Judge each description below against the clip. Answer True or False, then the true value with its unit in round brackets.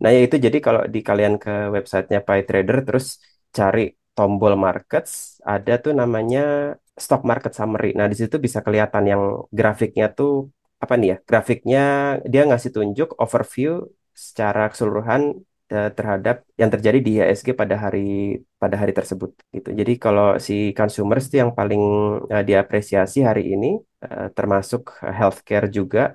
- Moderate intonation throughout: True (3.7 semitones)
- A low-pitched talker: True (105 Hz)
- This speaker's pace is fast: True (145 wpm)